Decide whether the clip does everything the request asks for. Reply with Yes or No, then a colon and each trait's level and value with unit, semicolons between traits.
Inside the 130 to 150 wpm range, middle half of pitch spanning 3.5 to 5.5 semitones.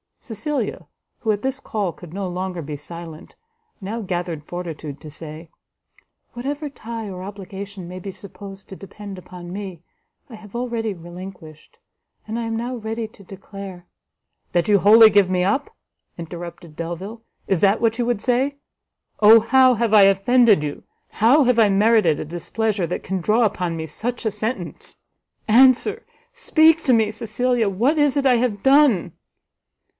No: average, 165 wpm; average, 4.6 semitones